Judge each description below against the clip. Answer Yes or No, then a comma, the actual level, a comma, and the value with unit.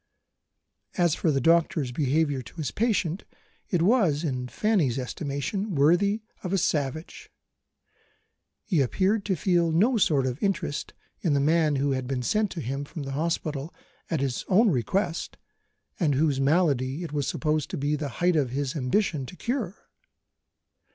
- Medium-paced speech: Yes, average, 160 wpm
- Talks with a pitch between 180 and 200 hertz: No, medium, 155 Hz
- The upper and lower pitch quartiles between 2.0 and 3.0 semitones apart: No, average, 4.7 semitones